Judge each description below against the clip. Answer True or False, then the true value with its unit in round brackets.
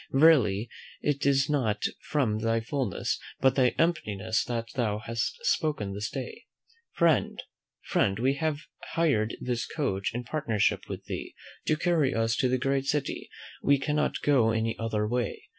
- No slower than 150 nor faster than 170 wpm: True (155 wpm)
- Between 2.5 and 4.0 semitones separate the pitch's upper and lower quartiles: False (4.6 semitones)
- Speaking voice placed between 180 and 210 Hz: False (125 Hz)